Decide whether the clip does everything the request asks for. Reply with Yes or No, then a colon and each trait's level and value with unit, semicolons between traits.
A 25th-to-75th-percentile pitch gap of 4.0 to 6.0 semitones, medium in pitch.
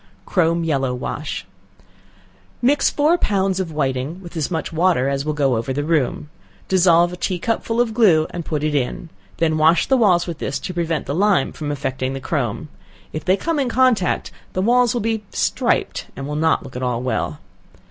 Yes: average, 5.1 semitones; medium, 165 Hz